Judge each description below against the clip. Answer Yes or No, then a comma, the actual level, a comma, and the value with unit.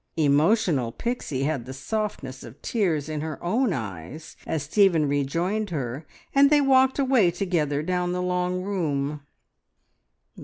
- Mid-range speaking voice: Yes, medium, 165 Hz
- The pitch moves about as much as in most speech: No, wide, 6.1 semitones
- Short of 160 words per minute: Yes, average, 140 wpm